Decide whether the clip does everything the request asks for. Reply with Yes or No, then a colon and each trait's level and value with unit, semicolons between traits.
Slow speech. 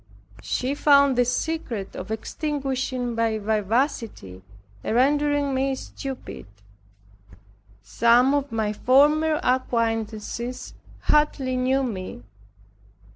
Yes: slow, 90 wpm